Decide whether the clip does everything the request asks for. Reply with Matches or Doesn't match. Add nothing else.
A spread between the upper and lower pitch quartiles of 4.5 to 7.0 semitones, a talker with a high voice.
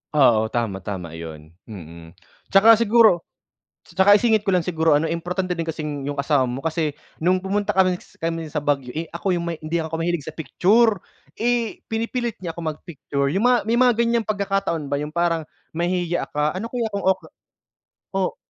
Doesn't match